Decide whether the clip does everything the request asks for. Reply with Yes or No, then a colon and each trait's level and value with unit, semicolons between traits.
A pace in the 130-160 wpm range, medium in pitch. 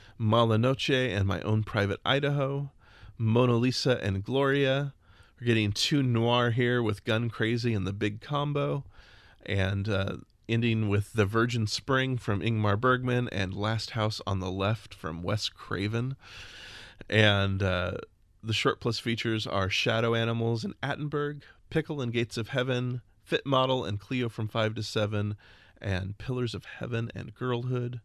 No: average, 150 wpm; low, 115 Hz